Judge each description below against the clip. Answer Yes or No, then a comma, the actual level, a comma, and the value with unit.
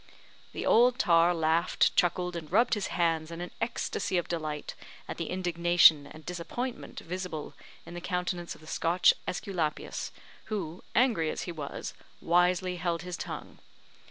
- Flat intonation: Yes, narrow, 1.7 semitones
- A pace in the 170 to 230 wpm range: No, average, 155 wpm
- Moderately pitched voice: Yes, medium, 175 Hz